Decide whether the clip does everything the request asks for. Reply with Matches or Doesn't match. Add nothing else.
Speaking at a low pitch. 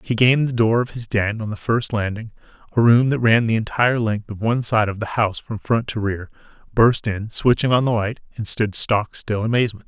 Matches